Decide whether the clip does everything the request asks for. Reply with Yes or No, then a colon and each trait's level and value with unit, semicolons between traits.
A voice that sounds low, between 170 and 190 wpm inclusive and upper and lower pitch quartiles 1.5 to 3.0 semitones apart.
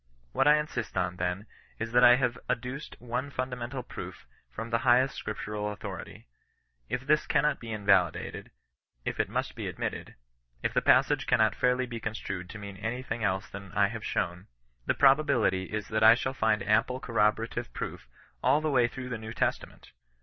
No: low, 115 Hz; average, 185 wpm; average, 3.4 semitones